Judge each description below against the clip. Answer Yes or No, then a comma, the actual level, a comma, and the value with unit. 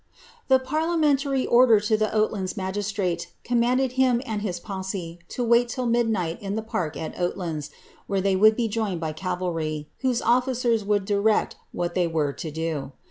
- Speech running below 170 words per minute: No, average, 175 wpm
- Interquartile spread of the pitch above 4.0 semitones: Yes, average, 5.3 semitones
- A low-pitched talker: No, high, 205 Hz